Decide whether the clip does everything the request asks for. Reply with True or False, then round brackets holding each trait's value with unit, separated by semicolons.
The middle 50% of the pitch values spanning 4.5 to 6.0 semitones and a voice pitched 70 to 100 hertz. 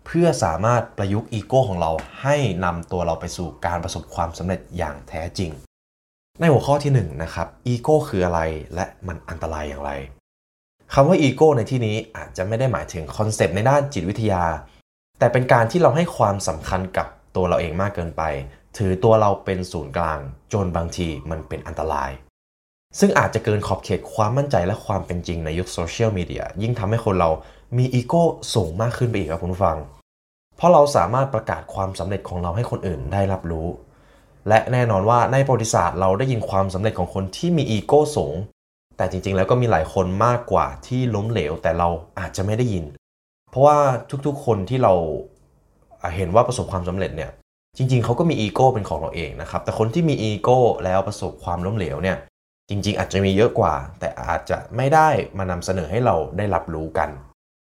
True (5.5 semitones; 95 Hz)